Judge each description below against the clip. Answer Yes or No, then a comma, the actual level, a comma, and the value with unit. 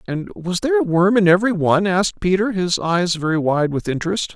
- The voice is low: No, medium, 180 Hz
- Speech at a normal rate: No, fast, 220 wpm